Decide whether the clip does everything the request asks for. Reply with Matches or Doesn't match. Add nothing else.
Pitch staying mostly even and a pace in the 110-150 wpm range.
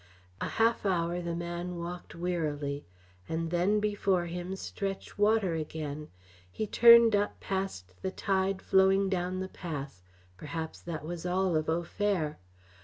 Doesn't match